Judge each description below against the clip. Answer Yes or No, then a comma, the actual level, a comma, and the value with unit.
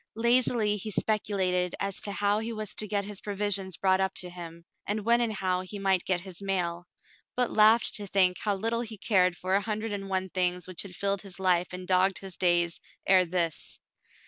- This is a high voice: Yes, high, 195 Hz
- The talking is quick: Yes, fast, 210 wpm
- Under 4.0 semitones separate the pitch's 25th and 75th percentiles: Yes, narrow, 2.4 semitones